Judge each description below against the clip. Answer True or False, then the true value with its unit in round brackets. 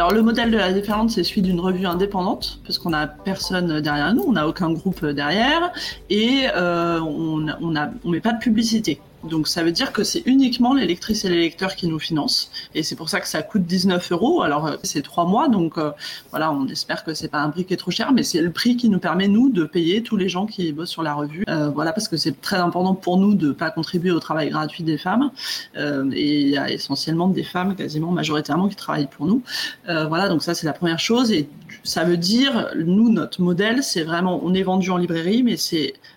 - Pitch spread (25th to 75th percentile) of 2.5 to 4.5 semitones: False (5.1 semitones)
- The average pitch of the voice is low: False (180 Hz)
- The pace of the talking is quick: True (240 wpm)